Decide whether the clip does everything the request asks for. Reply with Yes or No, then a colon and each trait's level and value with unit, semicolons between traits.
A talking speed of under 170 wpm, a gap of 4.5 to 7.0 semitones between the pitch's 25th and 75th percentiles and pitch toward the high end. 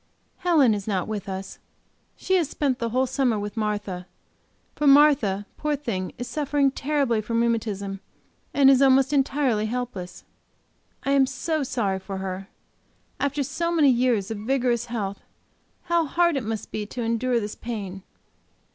Yes: average, 155 wpm; average, 5.1 semitones; high, 240 Hz